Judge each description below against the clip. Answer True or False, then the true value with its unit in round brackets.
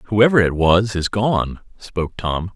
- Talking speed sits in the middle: True (165 wpm)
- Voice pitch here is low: True (95 Hz)